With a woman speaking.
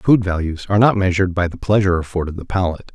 No: male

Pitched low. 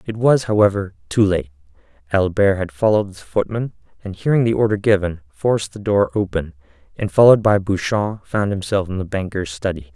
Yes: very low, 95 Hz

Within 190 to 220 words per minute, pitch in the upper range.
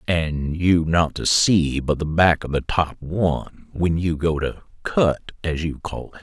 No: average, 200 wpm; very low, 80 Hz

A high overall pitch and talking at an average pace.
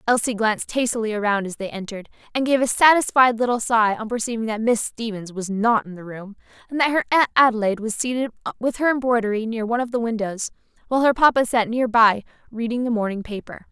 No: high, 230 Hz; fast, 210 wpm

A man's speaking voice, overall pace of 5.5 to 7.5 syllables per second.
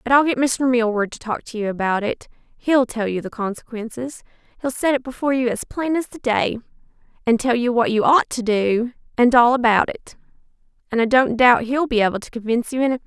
No: female; 6.0 syllables/s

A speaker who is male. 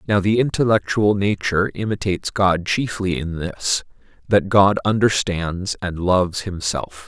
Yes: male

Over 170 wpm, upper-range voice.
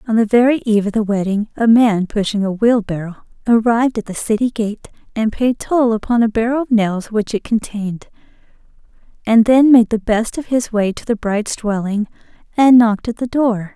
Yes: average, 195 wpm; high, 220 Hz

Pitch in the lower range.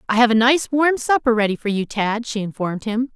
No: high, 230 Hz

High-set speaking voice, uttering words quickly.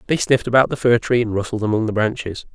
No: low, 115 Hz; fast, 260 wpm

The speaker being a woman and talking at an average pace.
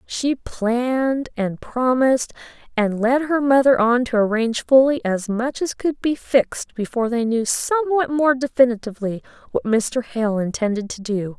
Yes: female; average, 160 wpm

